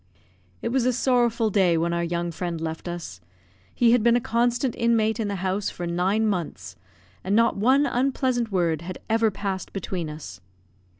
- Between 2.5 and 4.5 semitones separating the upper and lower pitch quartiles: No, average, 5.3 semitones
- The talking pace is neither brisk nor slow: Yes, average, 180 wpm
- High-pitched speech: Yes, high, 200 Hz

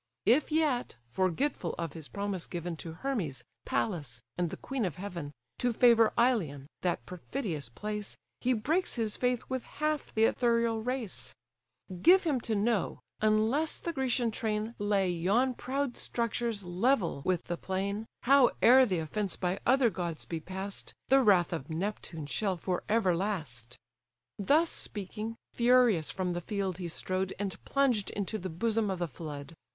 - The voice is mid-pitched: No, high, 205 Hz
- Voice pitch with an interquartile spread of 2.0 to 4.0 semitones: No, wide, 5.4 semitones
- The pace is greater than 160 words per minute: No, average, 155 wpm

